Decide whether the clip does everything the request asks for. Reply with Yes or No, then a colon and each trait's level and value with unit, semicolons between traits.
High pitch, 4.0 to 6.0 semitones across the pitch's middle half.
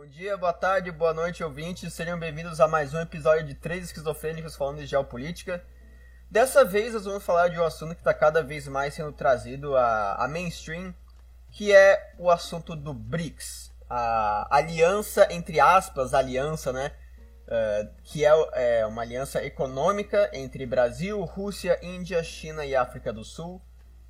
No: medium, 160 Hz; average, 5.1 semitones